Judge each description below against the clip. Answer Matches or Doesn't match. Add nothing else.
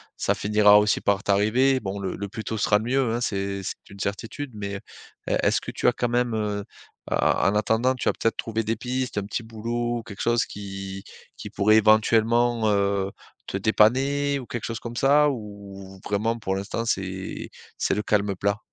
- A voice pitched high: Doesn't match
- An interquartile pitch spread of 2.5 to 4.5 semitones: Matches